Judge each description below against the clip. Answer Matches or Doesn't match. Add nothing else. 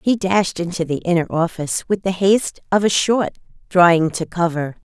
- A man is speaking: Doesn't match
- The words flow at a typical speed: Matches